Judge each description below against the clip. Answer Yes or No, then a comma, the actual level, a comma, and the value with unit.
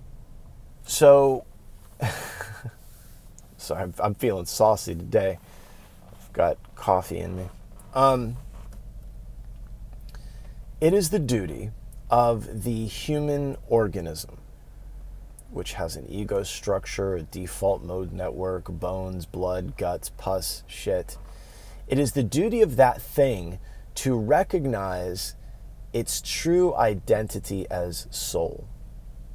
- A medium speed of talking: No, slow, 100 wpm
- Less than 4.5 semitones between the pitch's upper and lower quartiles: No, average, 5.1 semitones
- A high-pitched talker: No, low, 110 Hz